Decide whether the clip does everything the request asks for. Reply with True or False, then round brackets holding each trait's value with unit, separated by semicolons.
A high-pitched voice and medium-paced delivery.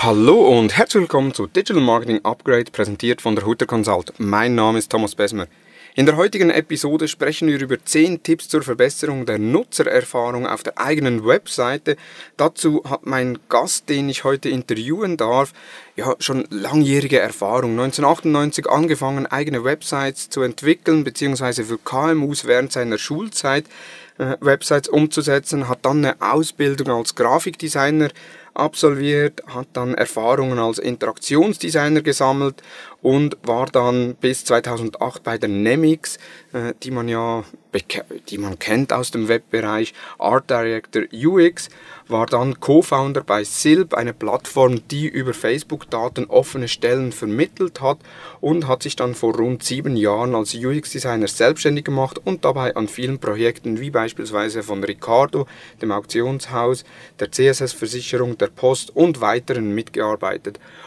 False (130 Hz; 140 wpm)